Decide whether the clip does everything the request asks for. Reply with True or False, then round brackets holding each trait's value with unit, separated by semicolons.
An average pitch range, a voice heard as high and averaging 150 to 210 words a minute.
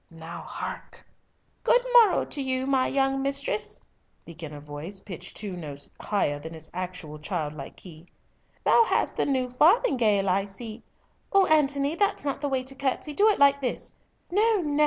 False (8.8 semitones; 255 Hz; 165 wpm)